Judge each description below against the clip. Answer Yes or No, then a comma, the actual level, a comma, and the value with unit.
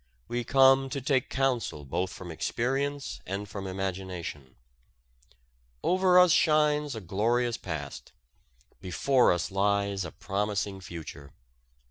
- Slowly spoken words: Yes, slow, 115 wpm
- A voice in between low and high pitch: No, low, 100 Hz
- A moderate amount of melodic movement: No, wide, 6.5 semitones